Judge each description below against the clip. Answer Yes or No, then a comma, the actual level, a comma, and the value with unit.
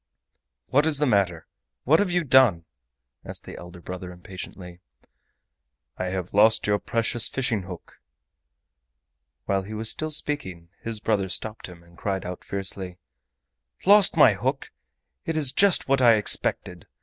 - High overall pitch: No, low, 105 Hz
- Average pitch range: No, wide, 6.6 semitones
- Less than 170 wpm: Yes, average, 145 wpm